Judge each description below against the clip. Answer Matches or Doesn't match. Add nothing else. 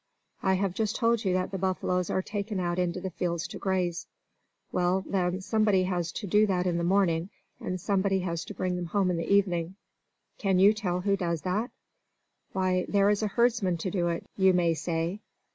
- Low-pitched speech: Doesn't match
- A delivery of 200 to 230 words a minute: Matches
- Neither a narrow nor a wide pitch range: Doesn't match